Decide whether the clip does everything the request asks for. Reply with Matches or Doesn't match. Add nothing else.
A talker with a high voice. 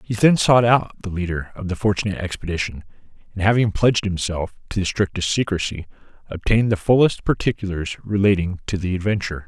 Doesn't match